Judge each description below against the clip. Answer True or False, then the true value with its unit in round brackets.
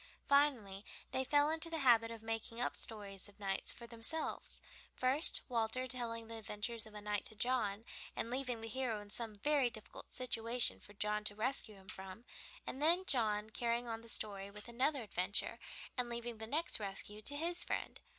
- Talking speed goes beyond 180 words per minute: True (190 wpm)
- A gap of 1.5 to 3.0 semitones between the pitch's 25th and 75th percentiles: False (3.4 semitones)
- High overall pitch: True (230 Hz)